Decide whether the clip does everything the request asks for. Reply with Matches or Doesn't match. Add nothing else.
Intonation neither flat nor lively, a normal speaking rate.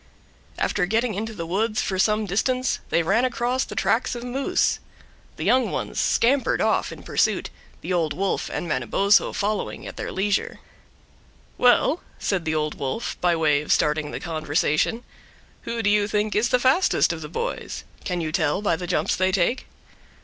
Doesn't match